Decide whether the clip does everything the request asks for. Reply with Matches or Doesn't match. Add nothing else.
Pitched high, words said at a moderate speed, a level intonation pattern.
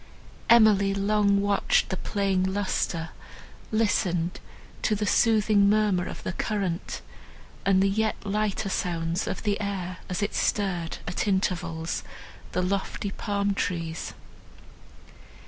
Doesn't match